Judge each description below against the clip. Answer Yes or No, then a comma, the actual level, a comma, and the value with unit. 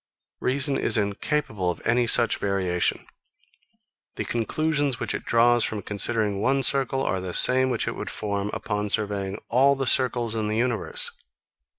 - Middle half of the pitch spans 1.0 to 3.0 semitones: No, average, 4.1 semitones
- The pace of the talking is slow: No, average, 160 wpm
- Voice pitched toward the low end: Yes, low, 115 Hz